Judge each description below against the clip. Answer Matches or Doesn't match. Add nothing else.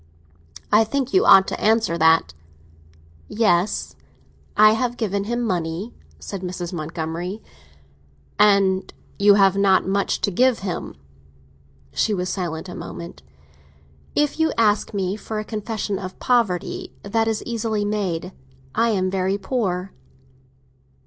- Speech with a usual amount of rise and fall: Matches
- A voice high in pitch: Matches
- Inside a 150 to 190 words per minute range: Doesn't match